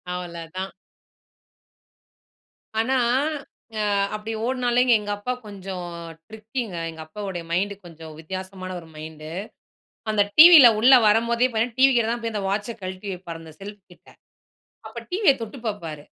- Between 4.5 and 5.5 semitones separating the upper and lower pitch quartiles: Yes, average, 4.8 semitones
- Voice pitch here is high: Yes, high, 205 Hz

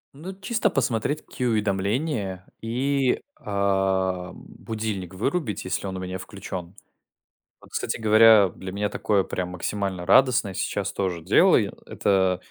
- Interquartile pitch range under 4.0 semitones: Yes, average, 3.3 semitones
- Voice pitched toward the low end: Yes, low, 100 Hz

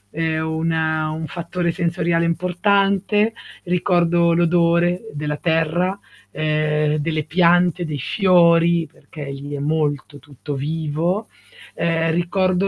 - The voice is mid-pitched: Yes, medium, 165 Hz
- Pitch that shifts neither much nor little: No, narrow, 2.3 semitones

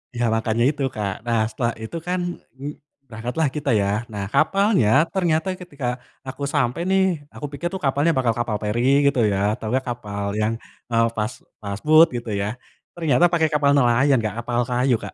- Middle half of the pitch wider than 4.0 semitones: Yes, average, 5.1 semitones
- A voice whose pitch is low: Yes, low, 125 Hz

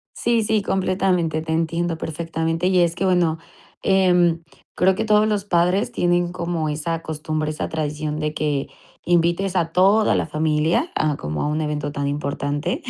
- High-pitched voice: No, medium, 165 Hz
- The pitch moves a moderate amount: Yes, average, 3.0 semitones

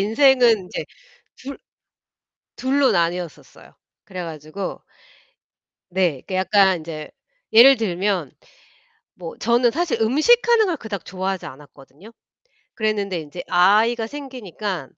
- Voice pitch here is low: No, high, 200 Hz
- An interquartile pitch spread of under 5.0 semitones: No, average, 5.3 semitones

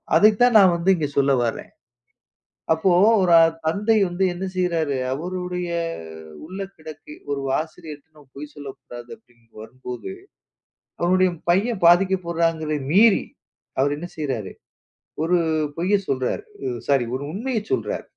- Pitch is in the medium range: Yes, medium, 170 Hz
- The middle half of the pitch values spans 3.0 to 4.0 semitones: No, average, 4.6 semitones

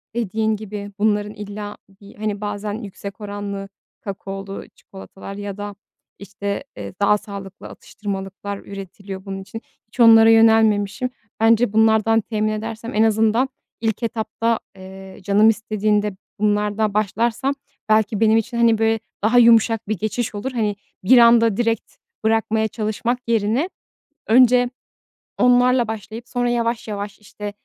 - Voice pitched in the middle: No, high, 215 Hz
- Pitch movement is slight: Yes, narrow, 1.9 semitones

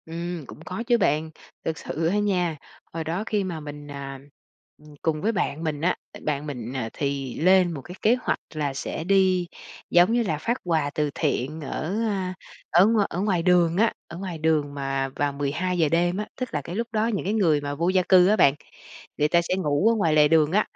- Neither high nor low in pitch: Yes, medium, 165 Hz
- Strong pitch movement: No, average, 4.2 semitones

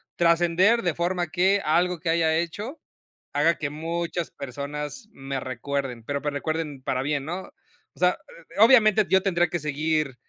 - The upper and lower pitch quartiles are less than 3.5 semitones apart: No, average, 3.8 semitones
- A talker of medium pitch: Yes, medium, 165 Hz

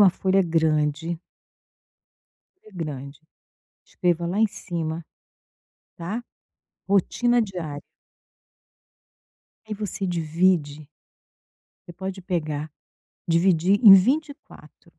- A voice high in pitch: No, medium, 175 Hz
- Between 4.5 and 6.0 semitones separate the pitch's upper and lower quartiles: No, average, 3.7 semitones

